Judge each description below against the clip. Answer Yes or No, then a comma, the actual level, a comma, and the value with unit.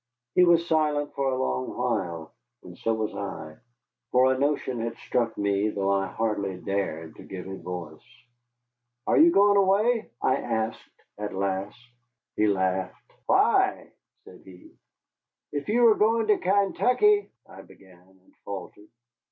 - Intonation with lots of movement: Yes, wide, 8.9 semitones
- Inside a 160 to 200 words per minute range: No, average, 150 wpm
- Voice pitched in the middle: No, low, 110 Hz